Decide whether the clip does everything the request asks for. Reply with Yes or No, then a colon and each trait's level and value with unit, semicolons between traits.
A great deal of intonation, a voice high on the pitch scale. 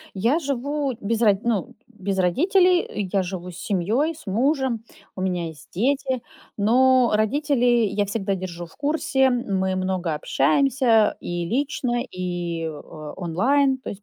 Yes: wide, 6.2 semitones; high, 220 Hz